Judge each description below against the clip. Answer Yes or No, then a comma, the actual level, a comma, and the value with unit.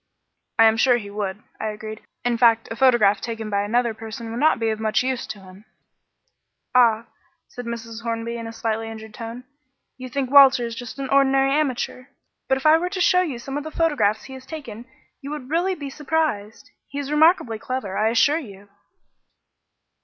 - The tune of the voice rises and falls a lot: No, average, 3.8 semitones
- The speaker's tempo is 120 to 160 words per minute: No, average, 200 wpm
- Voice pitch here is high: Yes, high, 235 Hz